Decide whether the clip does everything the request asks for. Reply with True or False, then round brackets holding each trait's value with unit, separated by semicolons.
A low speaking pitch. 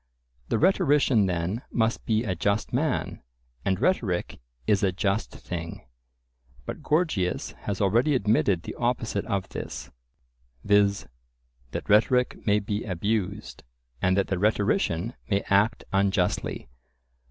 True (105 Hz)